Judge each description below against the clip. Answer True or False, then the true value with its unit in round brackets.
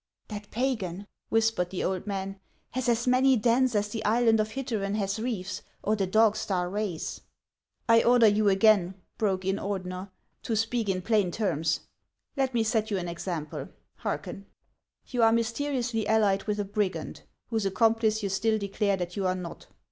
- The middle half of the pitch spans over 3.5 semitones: False (2.8 semitones)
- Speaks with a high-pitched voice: True (210 Hz)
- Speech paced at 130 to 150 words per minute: False (185 wpm)